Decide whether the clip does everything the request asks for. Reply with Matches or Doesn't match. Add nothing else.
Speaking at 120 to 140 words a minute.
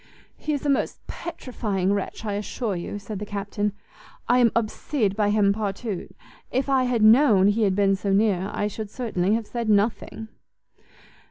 Doesn't match